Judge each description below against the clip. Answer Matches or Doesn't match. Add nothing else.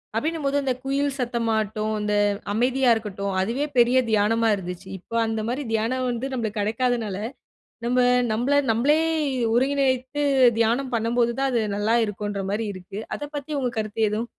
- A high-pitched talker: Matches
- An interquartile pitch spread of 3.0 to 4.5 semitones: Matches